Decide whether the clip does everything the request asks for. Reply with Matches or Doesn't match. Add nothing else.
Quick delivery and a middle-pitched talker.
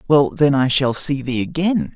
Matches